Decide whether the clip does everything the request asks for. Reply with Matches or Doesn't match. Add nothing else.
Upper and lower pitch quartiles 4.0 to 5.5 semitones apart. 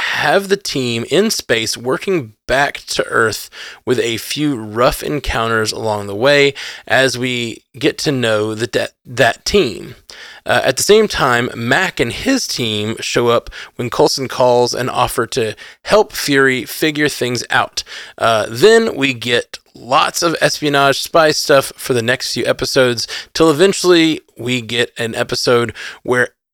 Matches